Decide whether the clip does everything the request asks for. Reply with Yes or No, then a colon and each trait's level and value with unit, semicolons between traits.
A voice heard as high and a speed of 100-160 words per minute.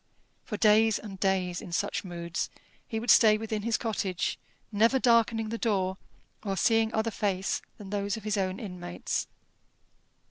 Yes: high, 210 Hz; average, 155 wpm